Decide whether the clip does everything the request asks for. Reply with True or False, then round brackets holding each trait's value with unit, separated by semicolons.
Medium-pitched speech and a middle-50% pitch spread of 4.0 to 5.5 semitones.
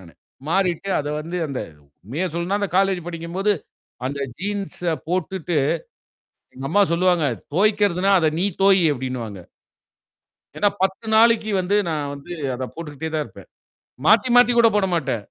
True (175 Hz; 4.7 semitones)